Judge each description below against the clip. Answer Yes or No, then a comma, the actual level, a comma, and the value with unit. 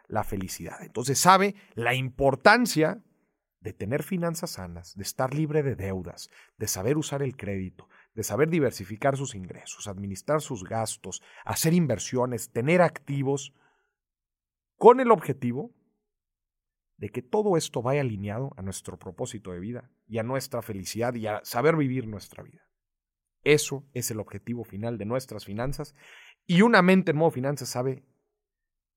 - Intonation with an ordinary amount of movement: No, wide, 6.3 semitones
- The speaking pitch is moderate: No, low, 125 Hz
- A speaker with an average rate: Yes, average, 145 wpm